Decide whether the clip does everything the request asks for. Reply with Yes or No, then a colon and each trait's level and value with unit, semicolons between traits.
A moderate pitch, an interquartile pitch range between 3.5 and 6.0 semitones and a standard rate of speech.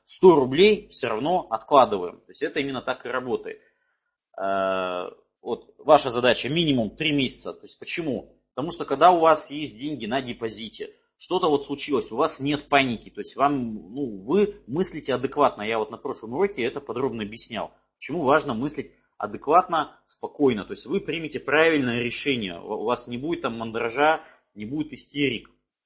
No: medium, 145 Hz; average, 5.3 semitones; fast, 170 wpm